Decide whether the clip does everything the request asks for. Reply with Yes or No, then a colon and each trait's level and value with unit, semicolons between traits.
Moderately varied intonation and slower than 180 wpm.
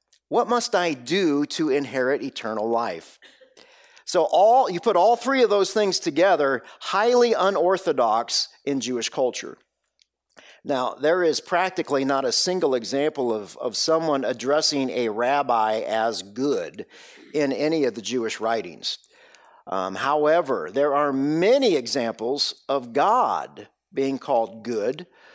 No: wide, 7.7 semitones; slow, 135 wpm